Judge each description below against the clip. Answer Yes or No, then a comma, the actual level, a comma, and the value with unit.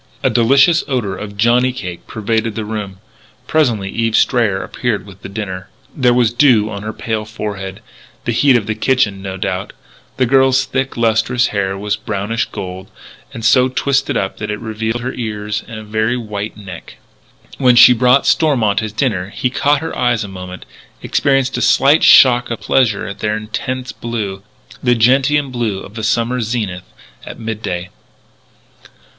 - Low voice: Yes, low, 110 Hz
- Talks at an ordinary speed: Yes, average, 170 wpm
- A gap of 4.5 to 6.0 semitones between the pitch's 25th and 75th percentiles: No, average, 3.4 semitones